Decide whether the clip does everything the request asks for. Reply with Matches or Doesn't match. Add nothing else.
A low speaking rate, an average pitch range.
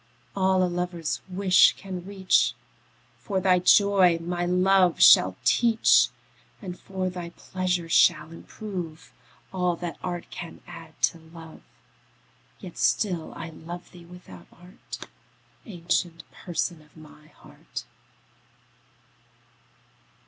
Doesn't match